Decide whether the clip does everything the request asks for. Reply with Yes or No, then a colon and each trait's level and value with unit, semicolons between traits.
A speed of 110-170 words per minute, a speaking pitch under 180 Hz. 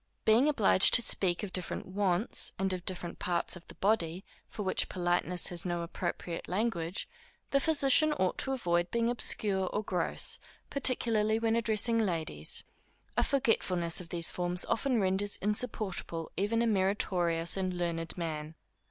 No: average, 150 wpm; high, 190 Hz